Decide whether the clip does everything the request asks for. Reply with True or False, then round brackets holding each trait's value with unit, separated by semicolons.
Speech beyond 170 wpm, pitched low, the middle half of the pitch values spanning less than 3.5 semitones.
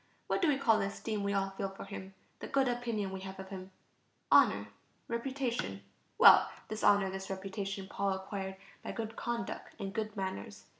False (185 wpm; 195 Hz; 2.8 semitones)